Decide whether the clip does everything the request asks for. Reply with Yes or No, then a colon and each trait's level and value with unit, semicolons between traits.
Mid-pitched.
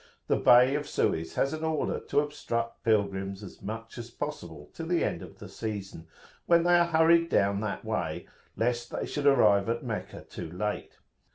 No: low, 115 Hz